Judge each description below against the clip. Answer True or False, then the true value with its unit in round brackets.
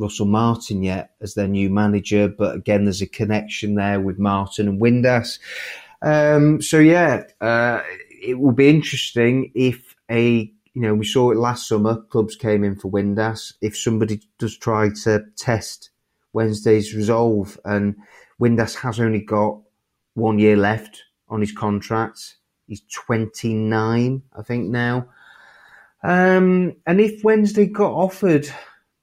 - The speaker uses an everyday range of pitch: True (3.0 semitones)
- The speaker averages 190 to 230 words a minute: False (145 wpm)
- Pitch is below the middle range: True (110 Hz)